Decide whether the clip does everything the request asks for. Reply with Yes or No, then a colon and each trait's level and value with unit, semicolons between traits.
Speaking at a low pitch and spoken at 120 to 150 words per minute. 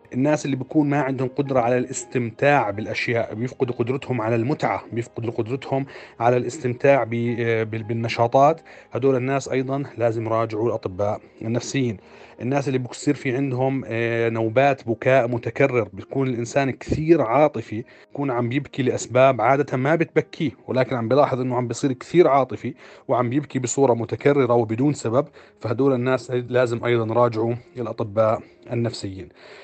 Yes: low, 125 Hz; average, 130 wpm